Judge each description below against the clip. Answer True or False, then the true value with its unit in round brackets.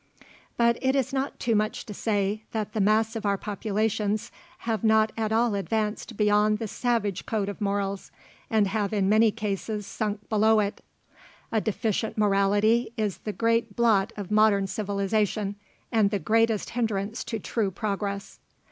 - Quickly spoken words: False (160 wpm)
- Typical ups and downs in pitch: False (1.7 semitones)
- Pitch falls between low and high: False (215 Hz)